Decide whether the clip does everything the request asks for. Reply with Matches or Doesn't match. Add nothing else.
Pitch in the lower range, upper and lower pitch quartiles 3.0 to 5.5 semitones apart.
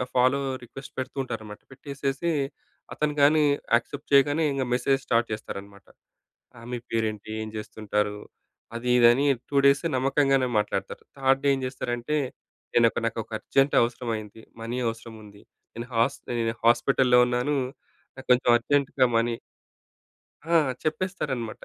Matches